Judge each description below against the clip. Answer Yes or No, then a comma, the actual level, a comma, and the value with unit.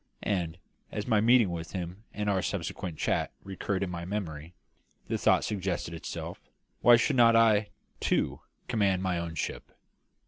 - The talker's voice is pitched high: No, very low, 95 Hz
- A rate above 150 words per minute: Yes, average, 160 wpm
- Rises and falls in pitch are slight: No, average, 3.6 semitones